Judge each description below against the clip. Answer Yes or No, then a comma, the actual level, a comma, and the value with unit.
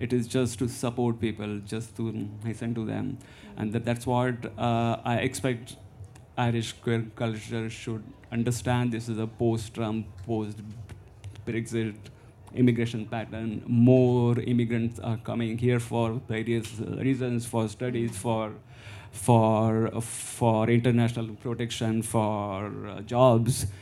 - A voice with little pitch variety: Yes, narrow, 1.6 semitones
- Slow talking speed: Yes, slow, 125 wpm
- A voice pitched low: Yes, low, 115 Hz